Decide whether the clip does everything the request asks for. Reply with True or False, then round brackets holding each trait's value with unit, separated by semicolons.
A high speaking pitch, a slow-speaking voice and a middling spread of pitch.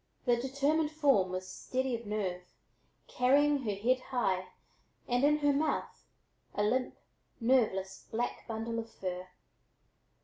True (240 Hz; 130 wpm; 4.8 semitones)